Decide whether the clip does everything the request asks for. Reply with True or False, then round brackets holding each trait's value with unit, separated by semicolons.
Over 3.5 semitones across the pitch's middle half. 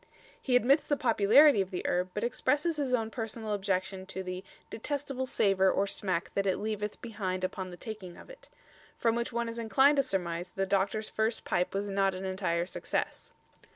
True (3.9 semitones)